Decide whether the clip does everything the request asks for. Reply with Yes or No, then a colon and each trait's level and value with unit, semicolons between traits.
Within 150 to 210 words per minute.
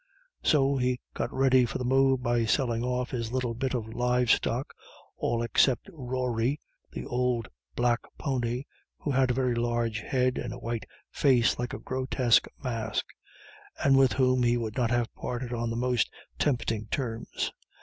Yes: average, 170 wpm